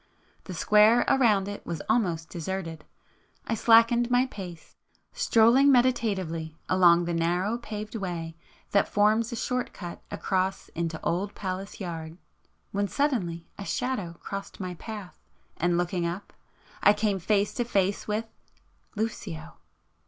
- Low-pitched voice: No, high, 195 Hz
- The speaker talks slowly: Yes, slow, 130 wpm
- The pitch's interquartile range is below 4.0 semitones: No, average, 4.5 semitones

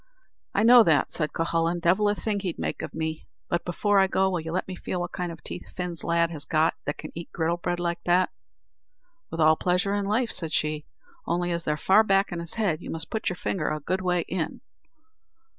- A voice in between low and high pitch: Yes, medium, 175 Hz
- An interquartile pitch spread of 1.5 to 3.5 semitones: Yes, narrow, 2.6 semitones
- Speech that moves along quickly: Yes, fast, 235 wpm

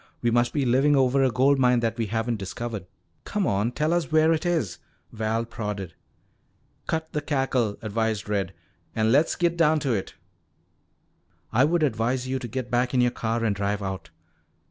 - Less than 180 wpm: No, average, 185 wpm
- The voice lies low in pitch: Yes, low, 120 Hz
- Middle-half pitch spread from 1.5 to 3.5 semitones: No, average, 4.3 semitones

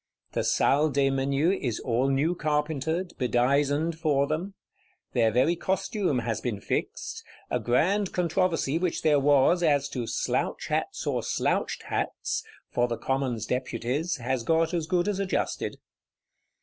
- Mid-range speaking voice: Yes, medium, 145 Hz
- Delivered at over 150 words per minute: No, average, 145 wpm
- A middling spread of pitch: Yes, average, 4.7 semitones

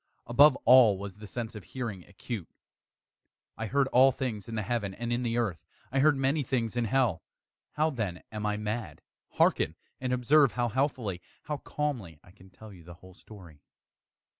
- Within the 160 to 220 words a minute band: Yes, average, 185 wpm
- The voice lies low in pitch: Yes, low, 115 Hz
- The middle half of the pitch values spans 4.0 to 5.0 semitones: Yes, average, 4.5 semitones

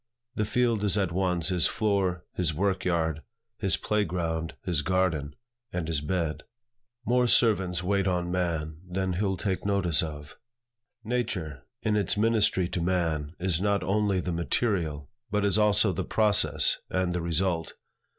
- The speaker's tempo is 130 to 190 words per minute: Yes, average, 155 wpm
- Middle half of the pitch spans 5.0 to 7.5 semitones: No, average, 3.5 semitones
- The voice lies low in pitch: Yes, very low, 90 Hz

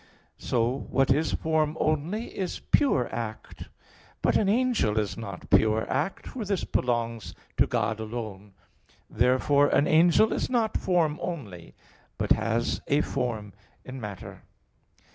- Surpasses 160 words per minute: No, slow, 135 wpm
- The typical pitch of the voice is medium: No, low, 130 Hz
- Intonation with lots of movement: Yes, wide, 7.1 semitones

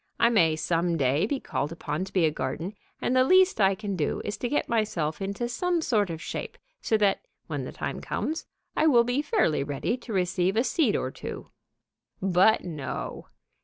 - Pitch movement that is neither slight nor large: No, wide, 6.5 semitones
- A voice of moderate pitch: No, high, 195 Hz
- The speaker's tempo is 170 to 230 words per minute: Yes, average, 200 wpm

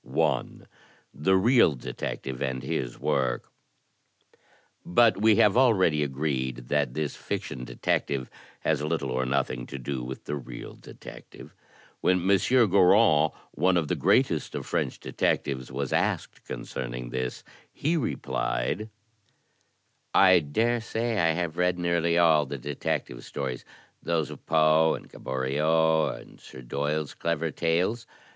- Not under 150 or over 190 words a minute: No, slow, 135 wpm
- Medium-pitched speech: No, very low, 75 Hz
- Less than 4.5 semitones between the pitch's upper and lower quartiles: No, average, 5.3 semitones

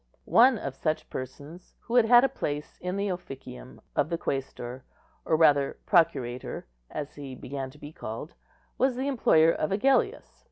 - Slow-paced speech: No, average, 165 wpm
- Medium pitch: Yes, medium, 155 Hz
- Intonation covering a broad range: Yes, wide, 8.2 semitones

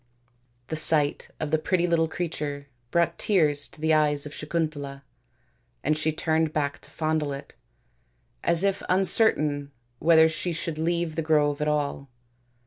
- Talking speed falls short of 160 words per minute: Yes, average, 150 wpm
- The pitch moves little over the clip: Yes, narrow, 2.0 semitones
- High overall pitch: No, medium, 155 Hz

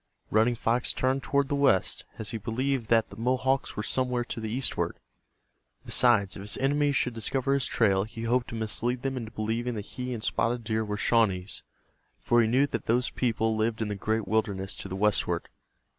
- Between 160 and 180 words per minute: No, average, 200 wpm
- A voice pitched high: No, low, 115 Hz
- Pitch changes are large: No, average, 2.7 semitones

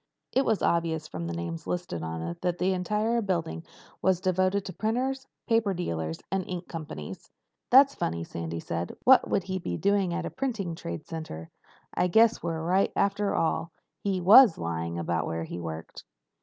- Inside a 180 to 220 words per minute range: Yes, average, 185 wpm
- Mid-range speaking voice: Yes, medium, 175 Hz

